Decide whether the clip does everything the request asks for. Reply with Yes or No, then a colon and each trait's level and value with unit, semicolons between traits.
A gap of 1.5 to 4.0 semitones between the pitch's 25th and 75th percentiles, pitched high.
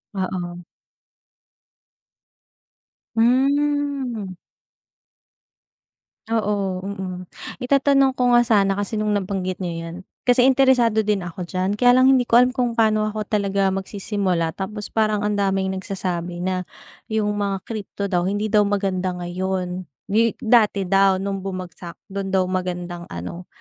Yes: average, 3.4 semitones; high, 200 Hz